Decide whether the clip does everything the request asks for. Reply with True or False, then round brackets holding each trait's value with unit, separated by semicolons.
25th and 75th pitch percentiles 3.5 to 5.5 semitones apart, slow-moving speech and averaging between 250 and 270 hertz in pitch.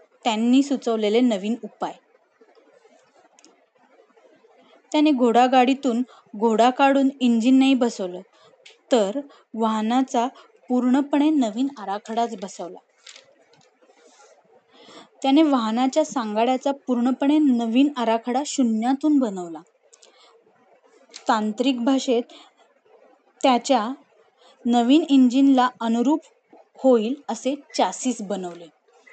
False (3.1 semitones; 70 wpm; 255 Hz)